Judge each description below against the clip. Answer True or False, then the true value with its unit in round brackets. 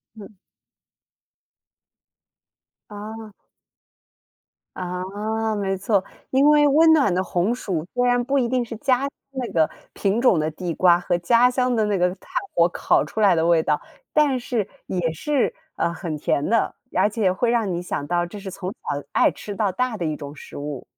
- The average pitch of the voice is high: True (205 Hz)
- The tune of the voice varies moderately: False (5.7 semitones)